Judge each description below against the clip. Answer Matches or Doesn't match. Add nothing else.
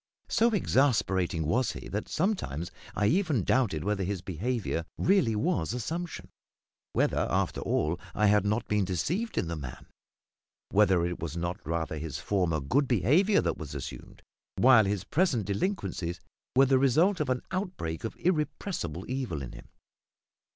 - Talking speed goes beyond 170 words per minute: Doesn't match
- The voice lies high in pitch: Doesn't match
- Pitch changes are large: Matches